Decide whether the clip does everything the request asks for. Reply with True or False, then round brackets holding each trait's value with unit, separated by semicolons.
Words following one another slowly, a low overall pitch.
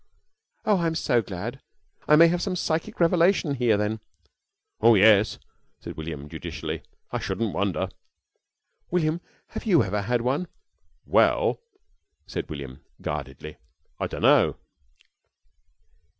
True (120 wpm; 120 Hz)